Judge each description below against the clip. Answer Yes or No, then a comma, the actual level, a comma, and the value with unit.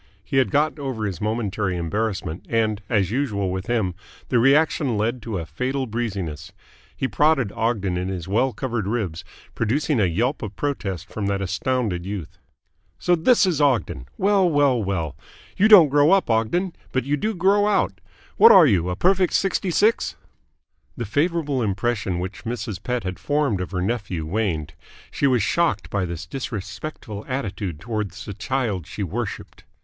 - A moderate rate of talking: Yes, average, 170 wpm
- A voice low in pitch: Yes, low, 115 Hz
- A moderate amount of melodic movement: No, wide, 6.7 semitones